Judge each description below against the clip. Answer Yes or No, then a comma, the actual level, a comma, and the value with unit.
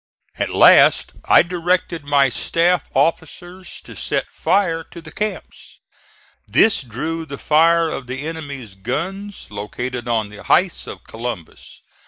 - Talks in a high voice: No, medium, 160 Hz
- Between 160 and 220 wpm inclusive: No, slow, 135 wpm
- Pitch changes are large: Yes, wide, 5.7 semitones